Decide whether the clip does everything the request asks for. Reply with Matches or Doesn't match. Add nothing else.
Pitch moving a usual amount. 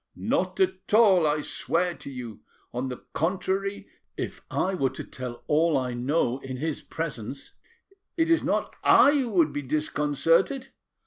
Doesn't match